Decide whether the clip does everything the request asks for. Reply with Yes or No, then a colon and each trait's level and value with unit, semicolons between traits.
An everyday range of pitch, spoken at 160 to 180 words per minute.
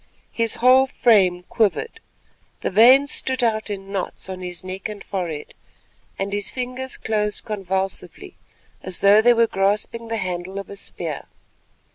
No: average, 3.4 semitones; average, 150 wpm